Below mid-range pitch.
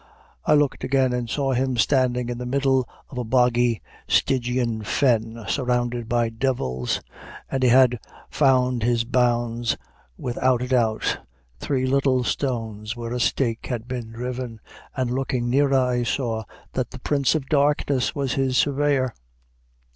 Yes: low, 125 Hz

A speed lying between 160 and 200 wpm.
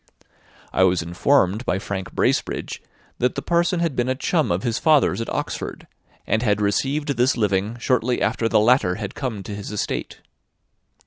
Yes: average, 175 wpm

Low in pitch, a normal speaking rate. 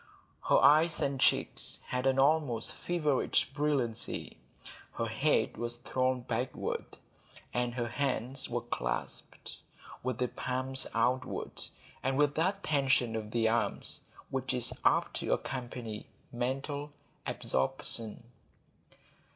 No: low, 130 Hz; slow, 115 wpm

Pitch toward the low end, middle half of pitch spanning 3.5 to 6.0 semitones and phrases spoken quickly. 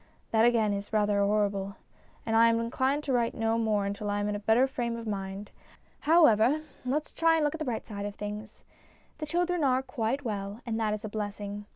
No: high, 225 Hz; average, 3.8 semitones; fast, 220 wpm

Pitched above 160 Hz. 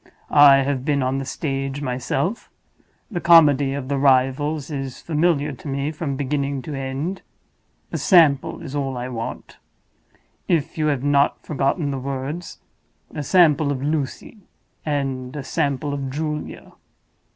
No: medium, 140 Hz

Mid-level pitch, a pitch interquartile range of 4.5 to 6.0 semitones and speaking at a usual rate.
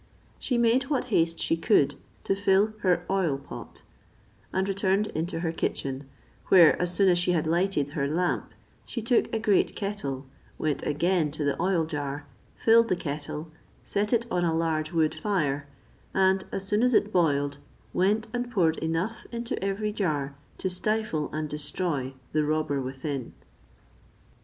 Yes: medium, 175 Hz; average, 5.1 semitones; average, 160 wpm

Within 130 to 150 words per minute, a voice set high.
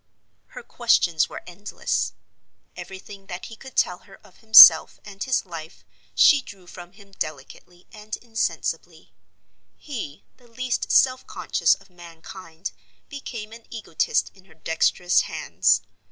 Yes: slow, 135 wpm; high, 195 Hz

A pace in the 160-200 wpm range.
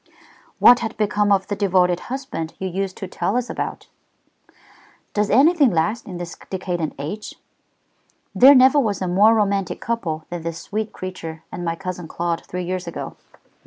Yes: average, 165 wpm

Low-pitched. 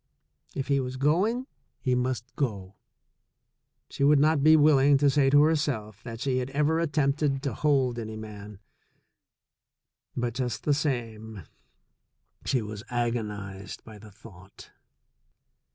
Yes: low, 130 Hz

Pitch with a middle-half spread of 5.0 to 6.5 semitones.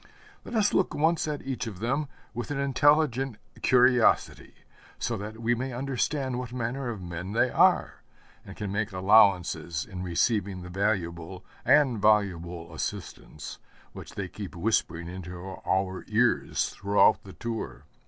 Yes: wide, 5.5 semitones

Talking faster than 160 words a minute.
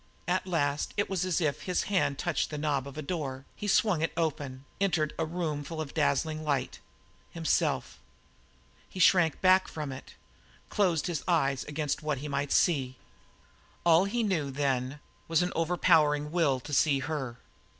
Yes: average, 170 wpm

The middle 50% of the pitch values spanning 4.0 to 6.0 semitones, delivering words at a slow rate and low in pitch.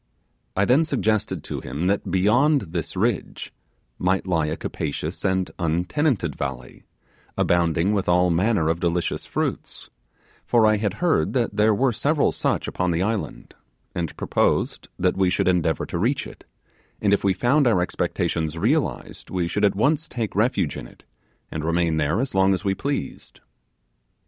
No: average, 4.9 semitones; average, 165 wpm; very low, 95 Hz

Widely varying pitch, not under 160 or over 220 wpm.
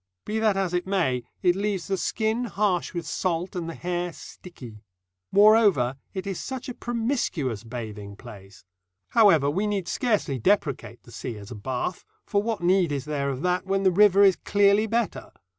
Yes: wide, 6.9 semitones; average, 180 wpm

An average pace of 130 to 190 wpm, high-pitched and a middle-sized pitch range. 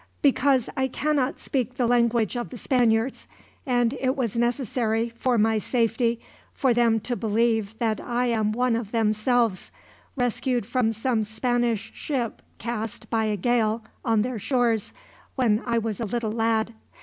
No: average, 155 wpm; high, 235 Hz; narrow, 1.9 semitones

